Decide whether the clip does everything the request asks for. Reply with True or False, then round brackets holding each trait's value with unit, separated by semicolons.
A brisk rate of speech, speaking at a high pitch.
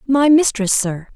False (155 wpm; 240 Hz)